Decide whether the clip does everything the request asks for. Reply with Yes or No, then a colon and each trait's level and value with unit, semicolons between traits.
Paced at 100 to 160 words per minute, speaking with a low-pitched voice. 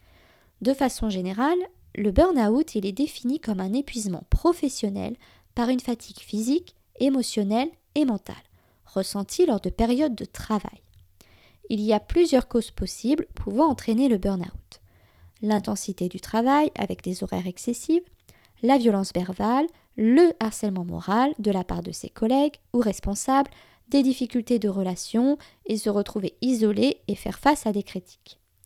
No: slow, 145 wpm; high, 225 Hz